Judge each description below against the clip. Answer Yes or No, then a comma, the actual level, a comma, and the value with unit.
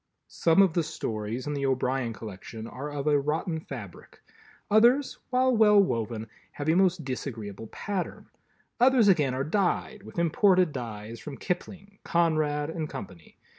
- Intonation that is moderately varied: No, wide, 7.0 semitones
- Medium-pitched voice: Yes, medium, 150 Hz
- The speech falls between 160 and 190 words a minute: No, average, 150 wpm